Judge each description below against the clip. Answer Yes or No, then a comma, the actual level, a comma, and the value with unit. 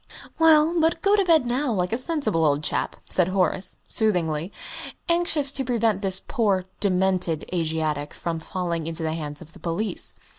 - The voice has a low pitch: No, medium, 185 Hz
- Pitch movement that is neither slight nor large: No, wide, 7.7 semitones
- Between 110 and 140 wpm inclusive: No, average, 170 wpm